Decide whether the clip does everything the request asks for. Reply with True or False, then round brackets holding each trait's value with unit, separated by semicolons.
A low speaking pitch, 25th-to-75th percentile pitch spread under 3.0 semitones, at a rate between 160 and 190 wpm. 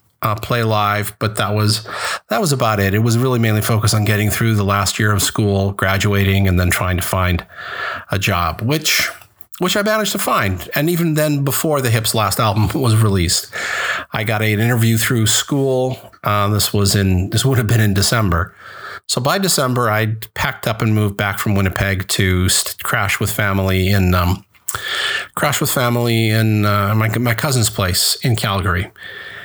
False (110 Hz; 3.3 semitones; 185 wpm)